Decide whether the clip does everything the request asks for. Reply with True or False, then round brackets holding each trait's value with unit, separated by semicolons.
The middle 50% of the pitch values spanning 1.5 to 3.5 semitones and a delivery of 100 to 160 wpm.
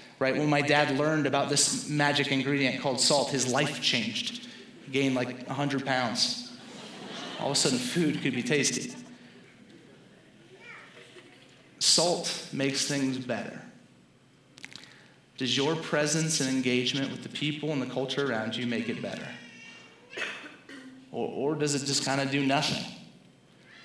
True (2.6 semitones; 140 wpm)